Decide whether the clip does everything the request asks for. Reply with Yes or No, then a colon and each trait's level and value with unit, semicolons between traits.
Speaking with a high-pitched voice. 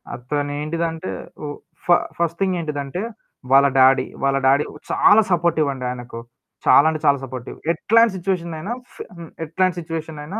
No: medium, 155 Hz